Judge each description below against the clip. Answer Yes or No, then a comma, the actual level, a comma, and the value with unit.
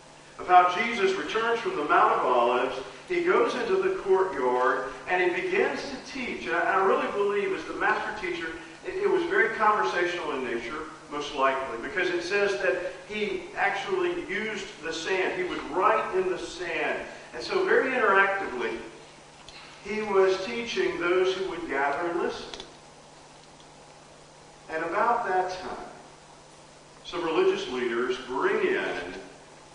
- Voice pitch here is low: No, high, 235 Hz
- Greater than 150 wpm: No, average, 145 wpm